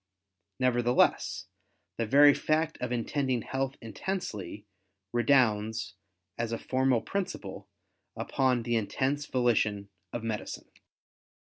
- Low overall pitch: Yes, low, 120 Hz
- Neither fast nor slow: No, slow, 100 wpm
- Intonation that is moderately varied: Yes, average, 3.2 semitones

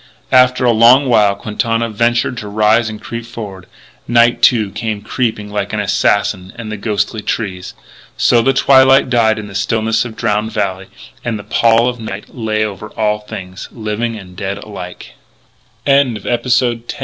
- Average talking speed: Yes, average, 150 wpm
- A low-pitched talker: Yes, low, 110 Hz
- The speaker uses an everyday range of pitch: No, narrow, 2.3 semitones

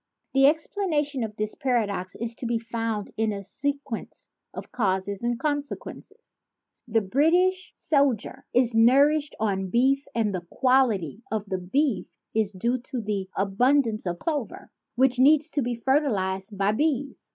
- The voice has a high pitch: Yes, high, 235 Hz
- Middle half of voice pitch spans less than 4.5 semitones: No, average, 5.2 semitones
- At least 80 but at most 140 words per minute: No, average, 155 wpm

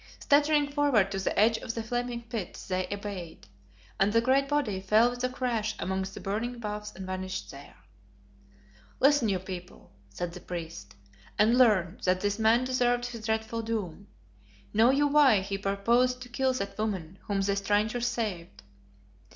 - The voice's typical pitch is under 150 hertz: No, high, 215 Hz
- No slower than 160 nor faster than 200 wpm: Yes, average, 165 wpm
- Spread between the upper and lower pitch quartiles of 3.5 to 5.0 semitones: Yes, average, 4.1 semitones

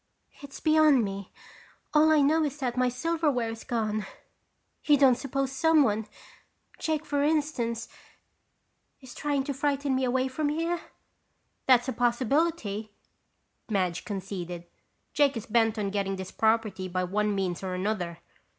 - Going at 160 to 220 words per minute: No, average, 140 wpm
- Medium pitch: No, high, 245 Hz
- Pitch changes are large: Yes, wide, 5.8 semitones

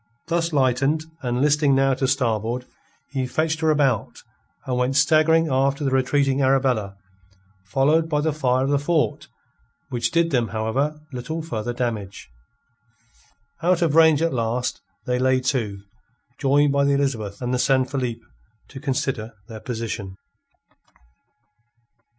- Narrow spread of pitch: No, average, 3.3 semitones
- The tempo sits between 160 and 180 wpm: No, average, 140 wpm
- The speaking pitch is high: No, low, 135 Hz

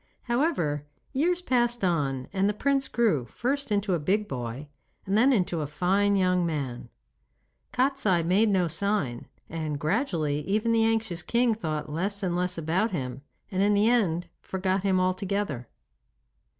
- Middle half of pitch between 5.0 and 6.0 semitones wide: Yes, wide, 5.6 semitones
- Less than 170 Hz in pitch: No, high, 190 Hz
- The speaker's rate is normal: Yes, average, 155 wpm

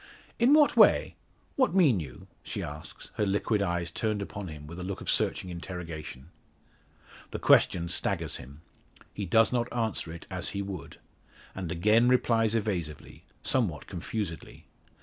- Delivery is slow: No, average, 150 wpm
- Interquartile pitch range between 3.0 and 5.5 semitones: Yes, average, 5.1 semitones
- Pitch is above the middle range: No, very low, 95 Hz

